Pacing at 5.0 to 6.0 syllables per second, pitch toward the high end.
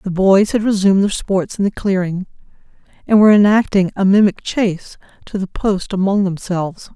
Yes: 5.4 syllables/s; high, 195 Hz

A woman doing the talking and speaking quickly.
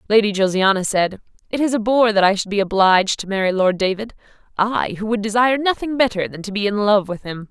Yes: female; fast, 230 wpm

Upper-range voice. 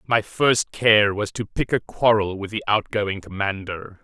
No: low, 105 Hz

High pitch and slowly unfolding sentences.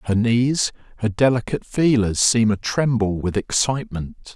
No: low, 115 Hz; slow, 125 wpm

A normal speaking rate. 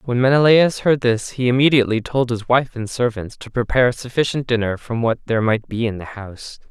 No: fast, 215 wpm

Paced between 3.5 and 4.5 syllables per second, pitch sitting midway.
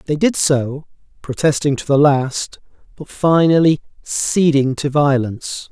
Yes: 4.1 syllables/s; medium, 145 Hz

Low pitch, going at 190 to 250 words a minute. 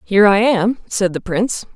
No: high, 205 Hz; fast, 205 wpm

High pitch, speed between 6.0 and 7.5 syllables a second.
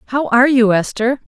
Yes: high, 245 Hz; 6.3 syllables/s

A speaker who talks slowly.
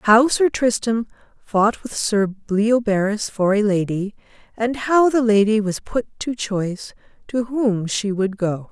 No: average, 160 wpm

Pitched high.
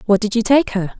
Yes: high, 225 Hz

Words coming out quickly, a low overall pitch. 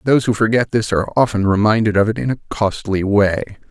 Yes: fast, 210 wpm; low, 110 Hz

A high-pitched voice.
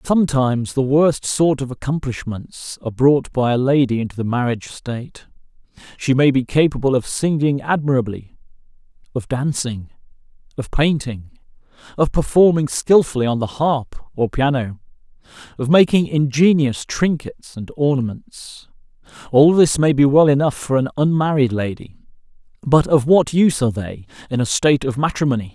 No: low, 135 Hz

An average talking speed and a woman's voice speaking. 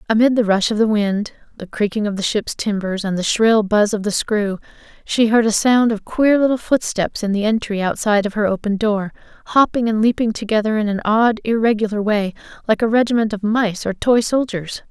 No: fast, 210 wpm; female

